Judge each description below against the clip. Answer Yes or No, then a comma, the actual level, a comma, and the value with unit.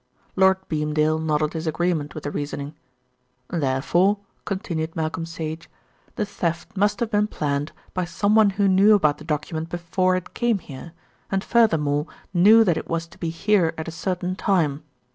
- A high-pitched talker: No, medium, 170 Hz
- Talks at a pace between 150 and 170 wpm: Yes, average, 165 wpm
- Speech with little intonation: No, average, 3.8 semitones